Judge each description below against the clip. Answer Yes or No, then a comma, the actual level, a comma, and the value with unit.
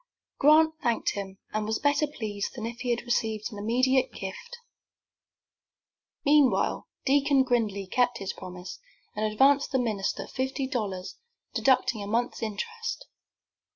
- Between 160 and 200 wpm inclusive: No, slow, 135 wpm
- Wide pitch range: No, average, 4.4 semitones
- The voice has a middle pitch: No, high, 240 Hz